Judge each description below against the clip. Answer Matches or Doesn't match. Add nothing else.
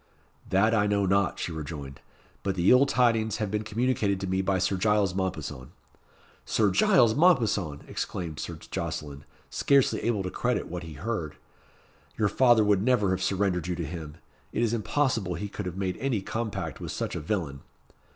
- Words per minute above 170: Matches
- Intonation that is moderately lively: Matches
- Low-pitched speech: Matches